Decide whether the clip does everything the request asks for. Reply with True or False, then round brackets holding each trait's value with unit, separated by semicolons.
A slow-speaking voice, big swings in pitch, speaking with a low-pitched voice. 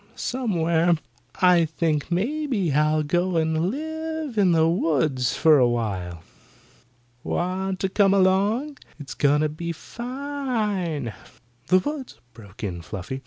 False (120 wpm; 6.2 semitones; 175 Hz)